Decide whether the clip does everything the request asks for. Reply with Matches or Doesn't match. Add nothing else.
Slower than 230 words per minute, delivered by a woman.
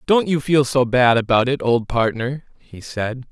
Doesn't match